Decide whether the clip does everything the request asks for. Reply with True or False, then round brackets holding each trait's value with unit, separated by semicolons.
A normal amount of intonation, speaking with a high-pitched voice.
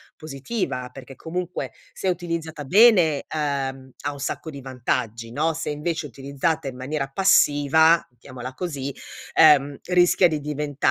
False (3.4 semitones; 145 Hz)